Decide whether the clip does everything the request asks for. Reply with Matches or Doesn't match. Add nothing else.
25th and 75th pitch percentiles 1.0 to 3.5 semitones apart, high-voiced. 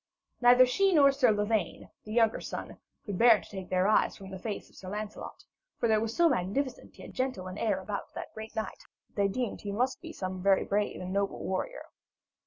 Doesn't match